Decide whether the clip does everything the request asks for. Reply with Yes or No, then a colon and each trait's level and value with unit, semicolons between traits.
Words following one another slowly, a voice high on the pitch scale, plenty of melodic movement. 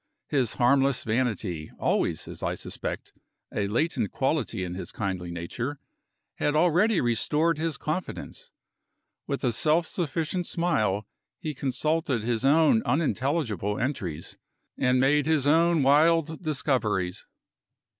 No: slow, 120 wpm; medium, 140 Hz; wide, 6.2 semitones